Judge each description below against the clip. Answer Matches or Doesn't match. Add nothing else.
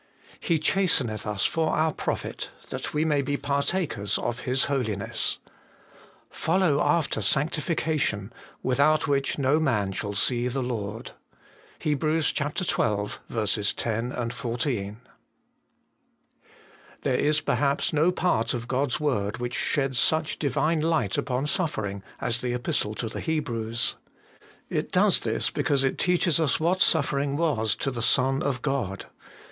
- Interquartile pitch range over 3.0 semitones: Matches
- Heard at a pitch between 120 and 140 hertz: Matches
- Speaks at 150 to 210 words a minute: Doesn't match